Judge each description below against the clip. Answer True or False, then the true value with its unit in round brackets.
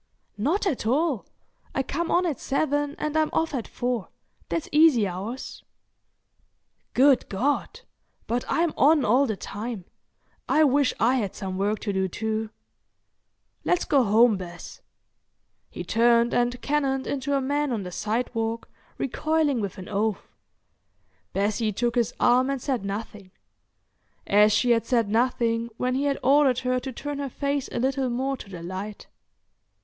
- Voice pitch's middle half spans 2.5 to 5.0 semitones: True (4.5 semitones)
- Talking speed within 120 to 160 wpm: True (155 wpm)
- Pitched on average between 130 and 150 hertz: False (245 Hz)